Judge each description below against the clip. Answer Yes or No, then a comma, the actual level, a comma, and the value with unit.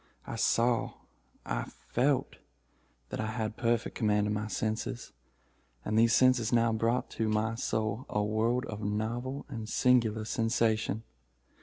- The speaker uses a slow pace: Yes, slow, 130 wpm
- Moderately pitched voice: No, low, 110 Hz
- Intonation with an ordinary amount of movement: No, narrow, 1.8 semitones